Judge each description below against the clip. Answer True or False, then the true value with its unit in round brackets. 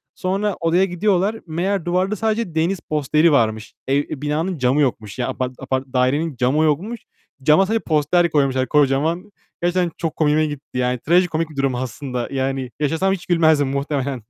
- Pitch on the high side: False (155 Hz)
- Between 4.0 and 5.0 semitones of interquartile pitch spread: True (4.7 semitones)